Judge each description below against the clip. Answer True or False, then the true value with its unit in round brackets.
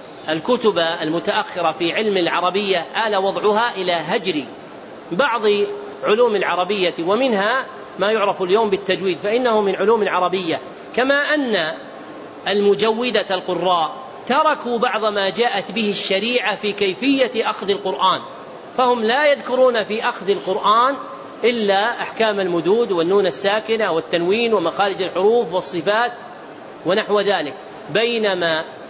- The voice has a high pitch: True (205 Hz)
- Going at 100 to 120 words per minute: True (110 wpm)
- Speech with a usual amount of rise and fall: True (3.7 semitones)